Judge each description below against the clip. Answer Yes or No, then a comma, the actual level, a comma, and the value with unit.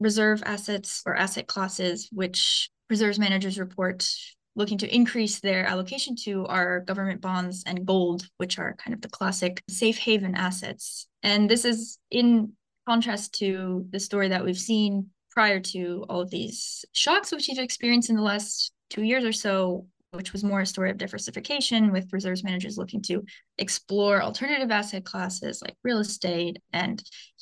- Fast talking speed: No, average, 165 wpm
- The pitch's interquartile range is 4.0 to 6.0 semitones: No, average, 2.9 semitones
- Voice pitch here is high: Yes, high, 200 Hz